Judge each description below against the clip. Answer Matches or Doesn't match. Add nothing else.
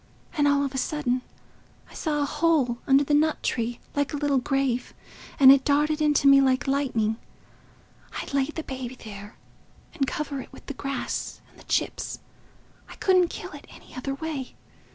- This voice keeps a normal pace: Matches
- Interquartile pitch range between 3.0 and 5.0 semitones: Doesn't match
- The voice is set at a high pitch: Matches